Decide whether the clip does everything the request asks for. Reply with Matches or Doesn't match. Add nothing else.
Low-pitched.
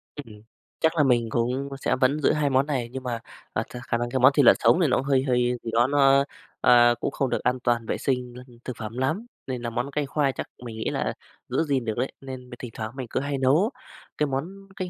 Matches